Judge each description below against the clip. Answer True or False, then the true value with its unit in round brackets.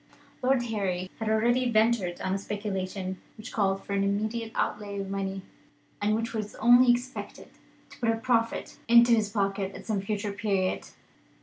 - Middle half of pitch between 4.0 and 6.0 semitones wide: False (2.8 semitones)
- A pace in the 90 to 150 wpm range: False (170 wpm)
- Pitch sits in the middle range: False (210 Hz)